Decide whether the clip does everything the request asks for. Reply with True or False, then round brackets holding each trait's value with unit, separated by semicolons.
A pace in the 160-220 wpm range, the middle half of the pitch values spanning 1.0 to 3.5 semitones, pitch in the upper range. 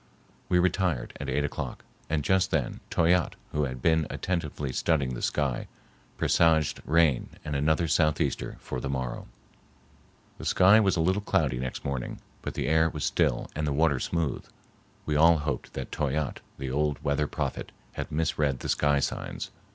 False (165 wpm; 2.9 semitones; 75 Hz)